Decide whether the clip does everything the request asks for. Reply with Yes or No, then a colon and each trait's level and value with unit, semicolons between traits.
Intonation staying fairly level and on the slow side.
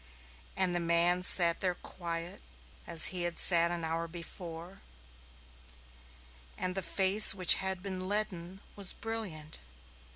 Yes: narrow, 2.1 semitones; slow, 130 wpm